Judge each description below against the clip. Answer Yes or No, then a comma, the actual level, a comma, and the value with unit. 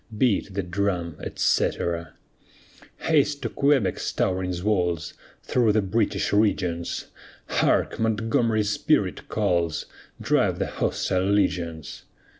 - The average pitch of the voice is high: No, low, 100 Hz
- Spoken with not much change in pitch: No, average, 4.1 semitones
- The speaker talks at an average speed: No, slow, 100 wpm